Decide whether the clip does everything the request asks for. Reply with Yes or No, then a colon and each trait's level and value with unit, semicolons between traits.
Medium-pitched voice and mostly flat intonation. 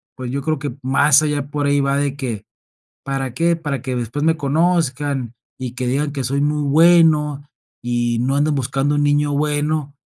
Yes: medium, 145 Hz; narrow, 2.1 semitones